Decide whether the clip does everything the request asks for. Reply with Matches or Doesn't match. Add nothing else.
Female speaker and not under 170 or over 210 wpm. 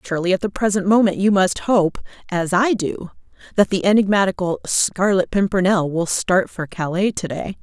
Matches